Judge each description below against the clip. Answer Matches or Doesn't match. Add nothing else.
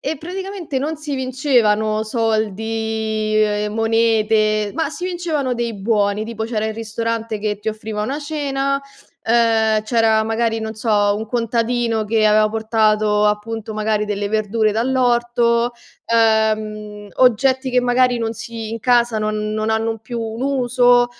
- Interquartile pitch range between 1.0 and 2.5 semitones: Matches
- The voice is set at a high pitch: Matches